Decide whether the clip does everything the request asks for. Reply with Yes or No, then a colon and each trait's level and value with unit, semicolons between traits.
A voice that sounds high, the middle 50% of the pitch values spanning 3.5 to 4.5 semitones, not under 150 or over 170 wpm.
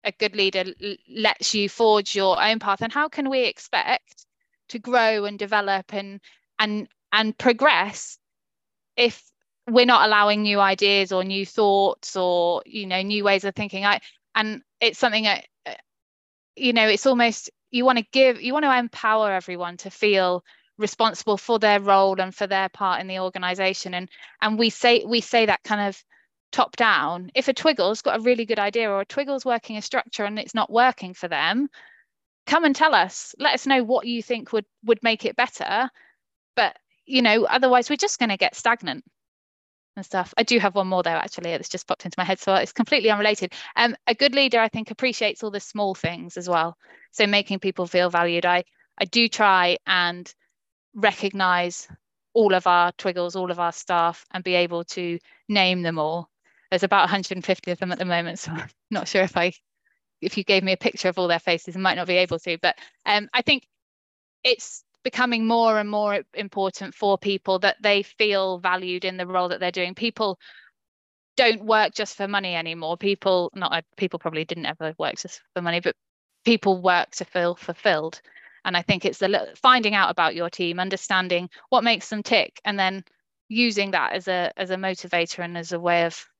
No: high, 200 Hz; average, 3.9 semitones; average, 200 wpm